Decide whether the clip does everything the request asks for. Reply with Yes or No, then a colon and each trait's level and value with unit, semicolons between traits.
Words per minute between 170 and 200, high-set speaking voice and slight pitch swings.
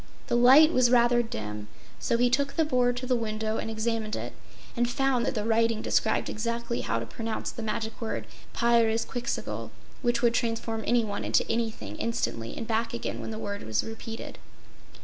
Yes: average, 180 wpm; high, 230 Hz; narrow, 1.6 semitones